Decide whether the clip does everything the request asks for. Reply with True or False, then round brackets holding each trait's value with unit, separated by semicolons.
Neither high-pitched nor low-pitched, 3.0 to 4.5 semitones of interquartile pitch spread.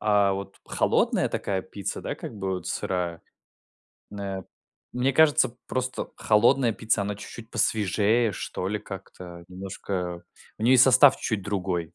False (100 Hz; 3.5 semitones)